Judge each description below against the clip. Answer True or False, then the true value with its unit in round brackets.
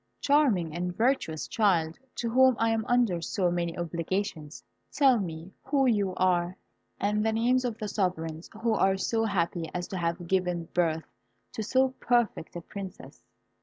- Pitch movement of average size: True (4.8 semitones)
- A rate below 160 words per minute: False (165 wpm)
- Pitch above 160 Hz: True (190 Hz)